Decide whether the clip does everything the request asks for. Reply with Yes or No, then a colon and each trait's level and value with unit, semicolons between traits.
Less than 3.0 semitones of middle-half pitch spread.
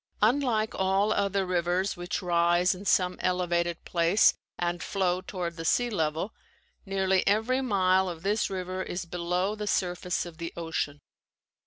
Yes: narrow, 2.4 semitones